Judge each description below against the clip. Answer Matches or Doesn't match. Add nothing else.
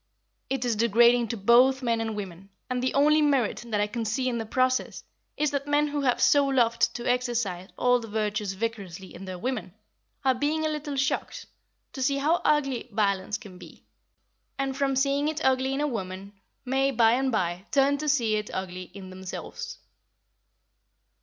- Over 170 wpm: Matches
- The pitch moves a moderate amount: Matches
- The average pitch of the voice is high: Matches